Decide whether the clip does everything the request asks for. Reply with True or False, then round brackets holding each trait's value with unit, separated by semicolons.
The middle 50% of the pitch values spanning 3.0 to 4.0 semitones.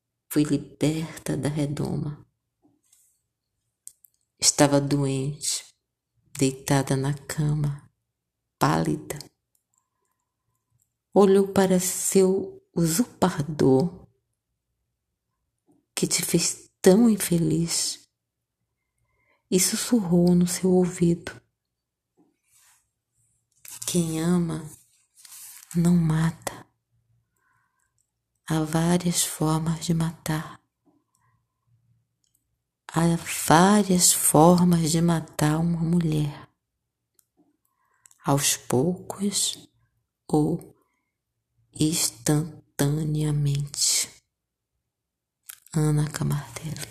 False (4.5 semitones)